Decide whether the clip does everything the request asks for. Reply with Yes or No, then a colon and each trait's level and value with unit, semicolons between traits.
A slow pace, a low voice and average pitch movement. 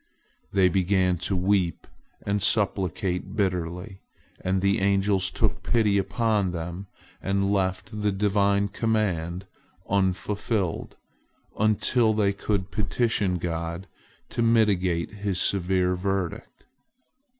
No: slow, 105 wpm; very low, 95 Hz; narrow, 2.2 semitones